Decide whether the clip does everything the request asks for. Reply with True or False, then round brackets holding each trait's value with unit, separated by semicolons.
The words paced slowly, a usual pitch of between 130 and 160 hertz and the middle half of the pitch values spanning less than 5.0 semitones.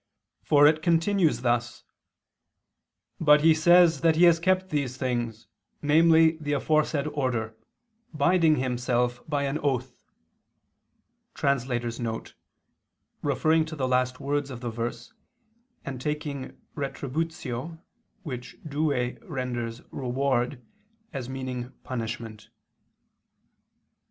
True (100 wpm; 140 Hz; 4.1 semitones)